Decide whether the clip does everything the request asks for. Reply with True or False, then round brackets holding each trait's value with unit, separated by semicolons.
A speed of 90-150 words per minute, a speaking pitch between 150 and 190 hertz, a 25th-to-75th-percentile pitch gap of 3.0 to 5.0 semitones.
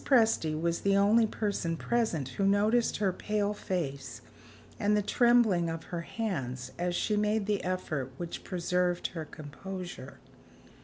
True (145 wpm; 185 Hz; 4.3 semitones)